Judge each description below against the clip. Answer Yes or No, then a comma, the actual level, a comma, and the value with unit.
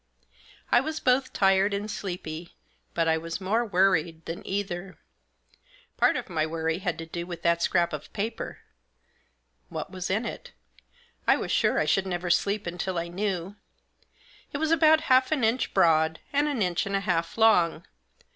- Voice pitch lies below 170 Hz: No, high, 190 Hz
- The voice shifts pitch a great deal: No, average, 4.3 semitones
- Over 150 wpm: Yes, average, 175 wpm